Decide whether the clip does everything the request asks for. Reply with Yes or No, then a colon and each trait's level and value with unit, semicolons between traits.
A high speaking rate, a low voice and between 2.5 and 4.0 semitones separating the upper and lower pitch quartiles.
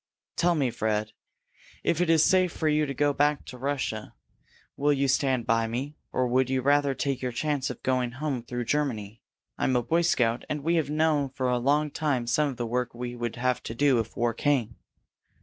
Yes: fast, 215 wpm; low, 130 Hz; average, 3.3 semitones